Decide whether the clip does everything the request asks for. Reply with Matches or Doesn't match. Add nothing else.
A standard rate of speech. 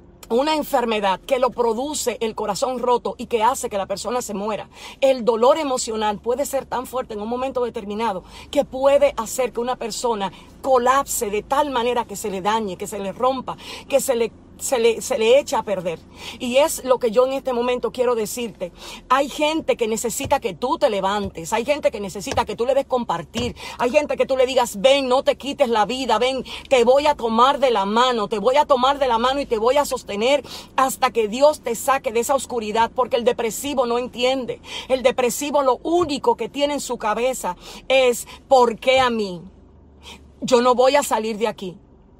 Doesn't match